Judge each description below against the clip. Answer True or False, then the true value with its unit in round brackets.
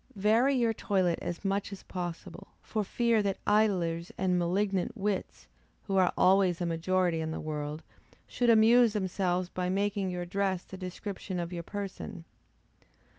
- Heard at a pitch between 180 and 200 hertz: True (190 Hz)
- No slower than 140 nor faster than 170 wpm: True (155 wpm)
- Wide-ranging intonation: False (2.7 semitones)